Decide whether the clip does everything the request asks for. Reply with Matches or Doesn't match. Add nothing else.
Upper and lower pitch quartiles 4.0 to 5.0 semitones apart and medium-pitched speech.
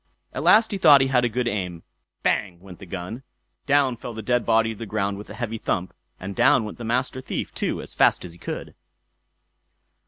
Doesn't match